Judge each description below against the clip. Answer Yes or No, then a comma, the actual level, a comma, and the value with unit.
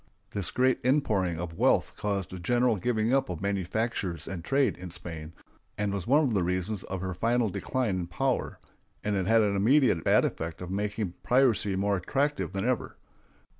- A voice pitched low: Yes, low, 100 Hz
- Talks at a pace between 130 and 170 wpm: No, average, 185 wpm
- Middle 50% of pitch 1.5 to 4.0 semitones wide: No, average, 5.0 semitones